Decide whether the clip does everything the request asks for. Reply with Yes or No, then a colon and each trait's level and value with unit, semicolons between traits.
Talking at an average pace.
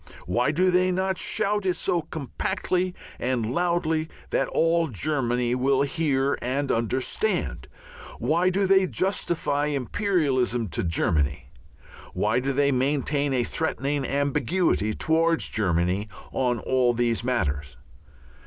No: slow, 120 wpm